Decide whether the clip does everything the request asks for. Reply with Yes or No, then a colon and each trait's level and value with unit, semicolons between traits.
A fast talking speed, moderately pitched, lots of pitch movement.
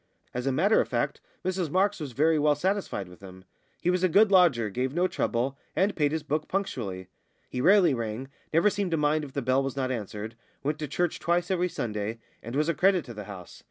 Yes: fast, 230 wpm; medium, 150 Hz; wide, 7.0 semitones